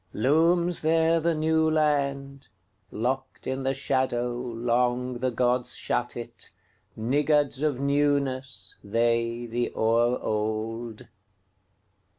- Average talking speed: No, slow, 85 wpm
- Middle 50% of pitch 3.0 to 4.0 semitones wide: Yes, average, 3.5 semitones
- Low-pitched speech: Yes, low, 125 Hz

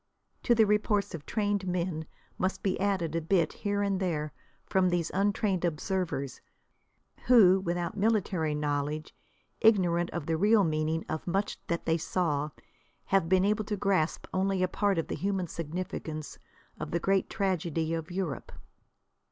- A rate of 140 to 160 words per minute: Yes, average, 155 wpm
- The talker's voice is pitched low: No, medium, 180 Hz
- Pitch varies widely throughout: No, average, 3.4 semitones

